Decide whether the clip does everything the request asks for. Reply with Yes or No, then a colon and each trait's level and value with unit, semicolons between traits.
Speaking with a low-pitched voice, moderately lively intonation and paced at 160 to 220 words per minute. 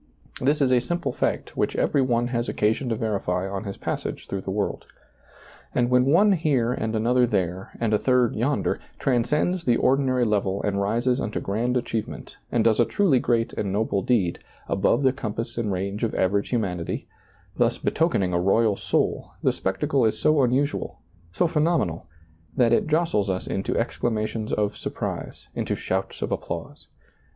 Yes: low, 115 Hz; average, 4.2 semitones; average, 175 wpm